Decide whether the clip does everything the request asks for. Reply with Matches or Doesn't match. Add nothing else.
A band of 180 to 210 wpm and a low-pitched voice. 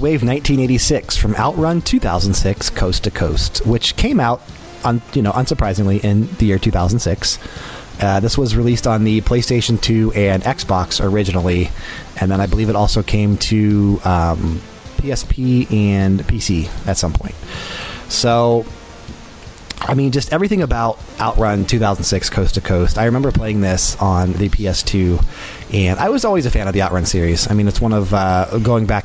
Doesn't match